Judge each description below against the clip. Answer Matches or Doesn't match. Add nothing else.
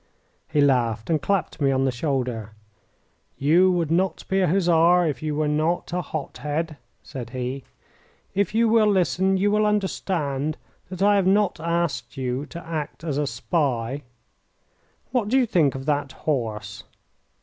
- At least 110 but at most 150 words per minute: Doesn't match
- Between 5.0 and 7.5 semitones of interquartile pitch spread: Matches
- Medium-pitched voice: Matches